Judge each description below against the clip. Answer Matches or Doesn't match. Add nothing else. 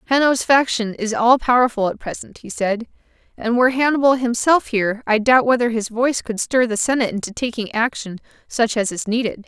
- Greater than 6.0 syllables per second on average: Doesn't match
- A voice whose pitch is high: Matches